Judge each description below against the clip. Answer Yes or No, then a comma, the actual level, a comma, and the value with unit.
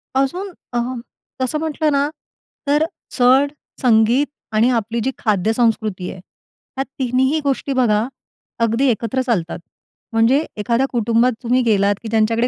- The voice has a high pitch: Yes, high, 240 Hz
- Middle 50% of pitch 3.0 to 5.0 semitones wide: Yes, average, 3.3 semitones